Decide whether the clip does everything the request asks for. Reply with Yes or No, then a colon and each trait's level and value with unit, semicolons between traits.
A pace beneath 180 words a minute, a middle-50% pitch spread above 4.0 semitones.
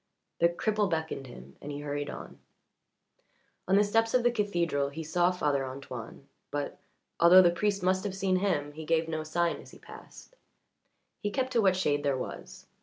No: average, 185 wpm; average, 5.2 semitones